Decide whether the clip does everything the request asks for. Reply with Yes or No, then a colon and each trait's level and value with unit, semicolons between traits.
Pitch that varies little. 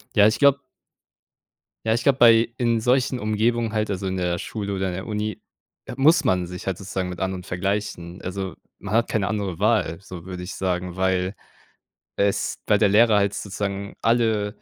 No: average, 3.2 semitones